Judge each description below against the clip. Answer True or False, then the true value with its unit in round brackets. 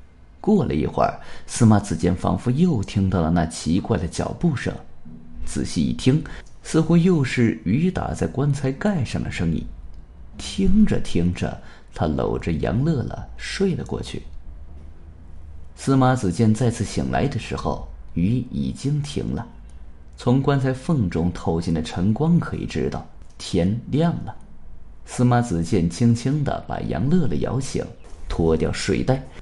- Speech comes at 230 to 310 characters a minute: False (210 characters per minute)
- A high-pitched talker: False (90 Hz)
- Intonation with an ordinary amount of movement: False (8.6 semitones)